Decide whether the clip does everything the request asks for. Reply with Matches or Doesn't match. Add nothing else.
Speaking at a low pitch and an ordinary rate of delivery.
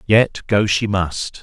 Matches